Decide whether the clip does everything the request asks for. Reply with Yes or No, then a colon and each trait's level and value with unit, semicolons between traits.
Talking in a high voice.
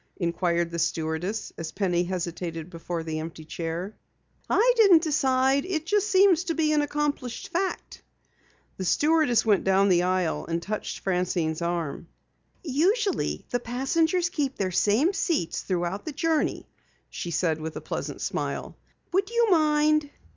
Yes: high, 220 Hz